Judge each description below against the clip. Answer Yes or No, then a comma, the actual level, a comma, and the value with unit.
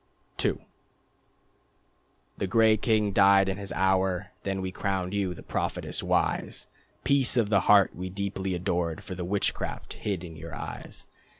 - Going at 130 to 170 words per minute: Yes, average, 155 wpm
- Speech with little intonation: Yes, narrow, 1.8 semitones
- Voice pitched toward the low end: Yes, very low, 95 Hz